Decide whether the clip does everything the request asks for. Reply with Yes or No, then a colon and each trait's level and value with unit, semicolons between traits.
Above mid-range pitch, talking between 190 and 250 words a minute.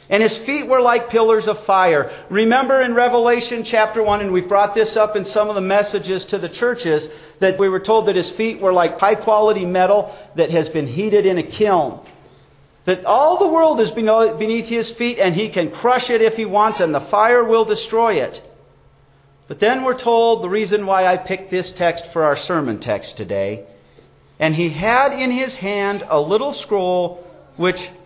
Yes: high, 210 Hz; average, 200 wpm